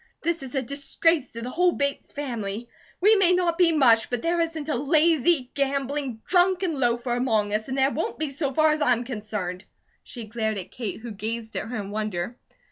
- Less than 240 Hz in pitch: No, very high, 265 Hz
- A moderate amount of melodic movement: No, wide, 5.7 semitones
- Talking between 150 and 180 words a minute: No, fast, 205 wpm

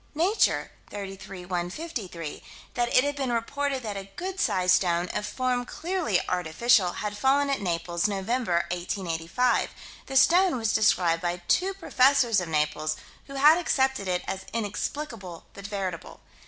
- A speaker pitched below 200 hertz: No, high, 210 Hz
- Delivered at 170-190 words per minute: No, average, 145 wpm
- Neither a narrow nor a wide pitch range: No, wide, 7.0 semitones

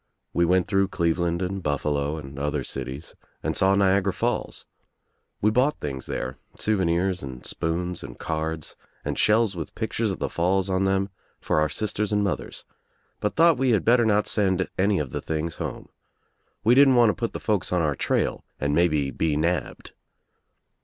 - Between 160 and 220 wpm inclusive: Yes, average, 180 wpm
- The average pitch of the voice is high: No, very low, 90 Hz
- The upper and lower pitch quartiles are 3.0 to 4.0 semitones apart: No, average, 5.0 semitones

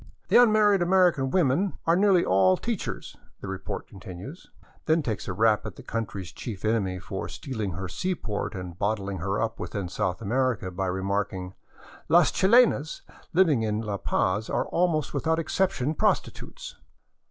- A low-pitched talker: Yes, low, 110 Hz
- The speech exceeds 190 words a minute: No, average, 165 wpm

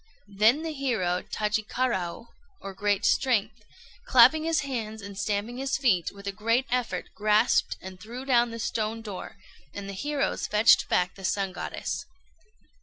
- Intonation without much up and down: No, average, 3.9 semitones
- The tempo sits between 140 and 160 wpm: Yes, average, 155 wpm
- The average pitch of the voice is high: Yes, high, 215 Hz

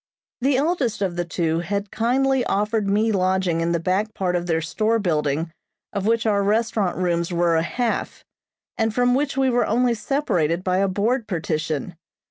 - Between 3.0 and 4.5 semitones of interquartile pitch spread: No, average, 5.1 semitones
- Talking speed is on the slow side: No, average, 180 wpm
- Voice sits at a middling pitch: No, high, 200 Hz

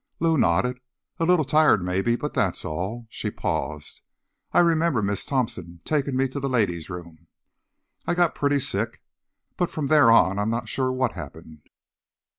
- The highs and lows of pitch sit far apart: Yes, wide, 8.1 semitones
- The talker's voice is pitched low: Yes, low, 120 Hz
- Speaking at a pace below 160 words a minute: No, average, 165 wpm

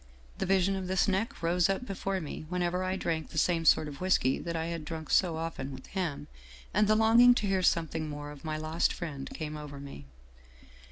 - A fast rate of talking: Yes, fast, 215 wpm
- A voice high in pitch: No, medium, 170 Hz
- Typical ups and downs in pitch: Yes, average, 3.6 semitones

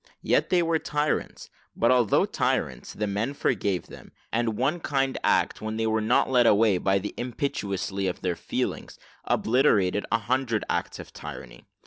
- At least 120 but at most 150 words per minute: No, average, 165 wpm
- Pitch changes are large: No, average, 4.7 semitones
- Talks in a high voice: No, low, 110 Hz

